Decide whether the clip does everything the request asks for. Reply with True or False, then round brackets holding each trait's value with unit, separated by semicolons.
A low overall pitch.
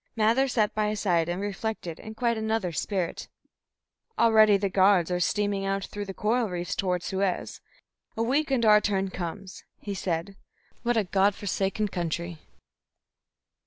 False (200 Hz)